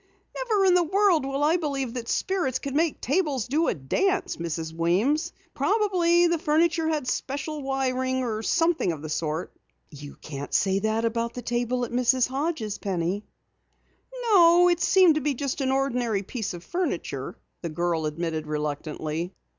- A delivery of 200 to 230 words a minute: No, average, 165 wpm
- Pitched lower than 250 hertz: No, very high, 260 Hz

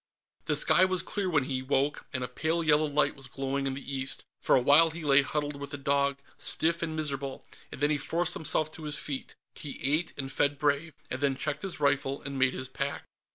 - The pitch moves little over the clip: Yes, narrow, 2.3 semitones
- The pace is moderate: No, fast, 230 wpm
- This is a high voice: No, medium, 145 Hz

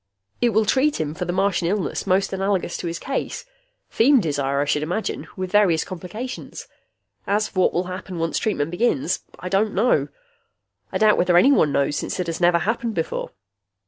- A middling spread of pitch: Yes, average, 4.2 semitones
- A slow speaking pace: No, average, 185 wpm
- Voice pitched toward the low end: No, medium, 185 Hz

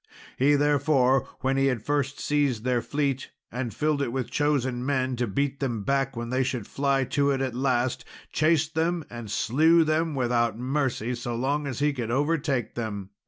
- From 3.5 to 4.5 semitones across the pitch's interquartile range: No, average, 3.0 semitones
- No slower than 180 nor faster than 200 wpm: Yes, average, 185 wpm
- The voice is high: No, low, 135 Hz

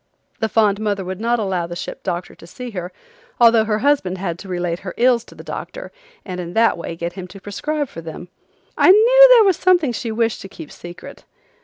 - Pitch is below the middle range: No, high, 205 Hz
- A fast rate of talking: Yes, fast, 220 wpm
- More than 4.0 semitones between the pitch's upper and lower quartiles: Yes, average, 5.2 semitones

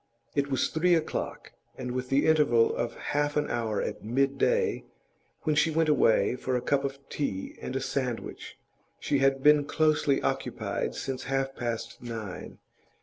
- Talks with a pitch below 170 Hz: Yes, low, 135 Hz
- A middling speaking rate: Yes, average, 160 wpm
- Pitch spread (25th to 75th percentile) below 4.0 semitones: Yes, average, 3.2 semitones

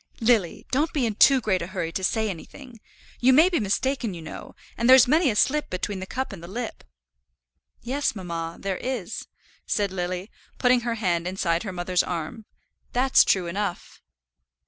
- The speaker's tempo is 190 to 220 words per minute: No, average, 180 wpm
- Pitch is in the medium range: No, high, 210 Hz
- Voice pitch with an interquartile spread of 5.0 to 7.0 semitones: Yes, wide, 5.6 semitones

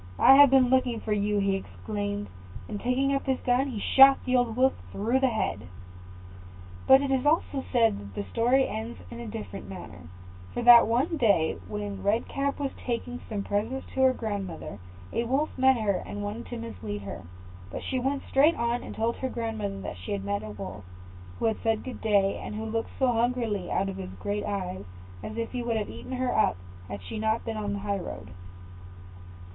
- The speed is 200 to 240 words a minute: Yes, fast, 205 wpm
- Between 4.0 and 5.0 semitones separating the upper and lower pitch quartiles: Yes, average, 4.7 semitones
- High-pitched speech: Yes, high, 220 Hz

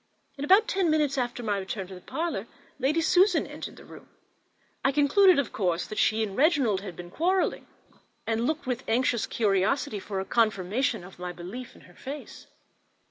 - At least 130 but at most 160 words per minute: No, average, 185 wpm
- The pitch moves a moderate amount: No, wide, 6.9 semitones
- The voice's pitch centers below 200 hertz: No, high, 240 Hz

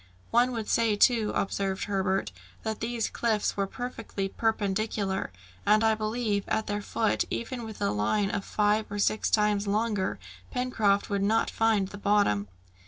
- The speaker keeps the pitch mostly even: Yes, narrow, 2.0 semitones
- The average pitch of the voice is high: Yes, high, 210 Hz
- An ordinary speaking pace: Yes, average, 160 wpm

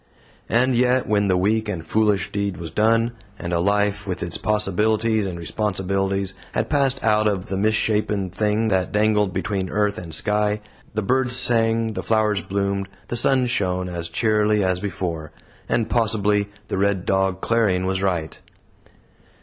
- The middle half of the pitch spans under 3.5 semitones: Yes, narrow, 2.6 semitones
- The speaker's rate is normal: Yes, average, 160 wpm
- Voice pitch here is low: Yes, low, 105 Hz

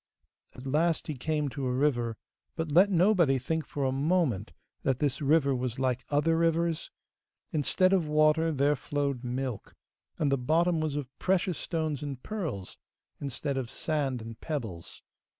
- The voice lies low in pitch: No, medium, 145 Hz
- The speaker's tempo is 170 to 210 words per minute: No, average, 160 wpm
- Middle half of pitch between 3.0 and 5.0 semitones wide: Yes, average, 3.8 semitones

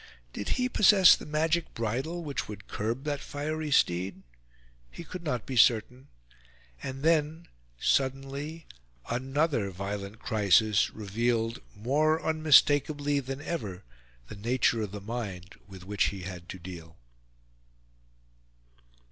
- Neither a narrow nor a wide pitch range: No, wide, 6.7 semitones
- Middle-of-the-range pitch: No, low, 125 Hz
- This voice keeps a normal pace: No, slow, 120 wpm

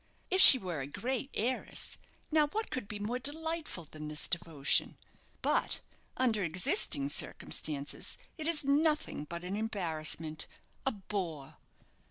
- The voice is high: Yes, high, 200 Hz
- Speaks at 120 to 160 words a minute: Yes, slow, 135 wpm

